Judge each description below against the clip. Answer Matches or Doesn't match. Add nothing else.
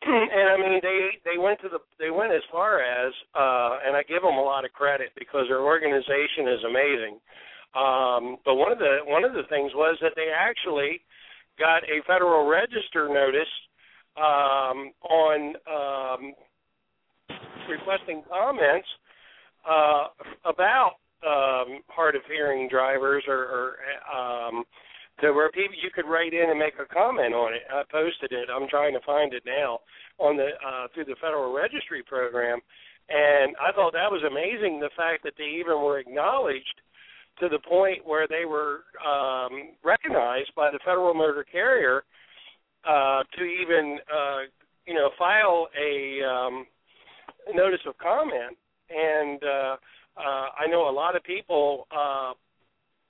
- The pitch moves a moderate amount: Matches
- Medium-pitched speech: Matches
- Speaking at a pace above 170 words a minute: Doesn't match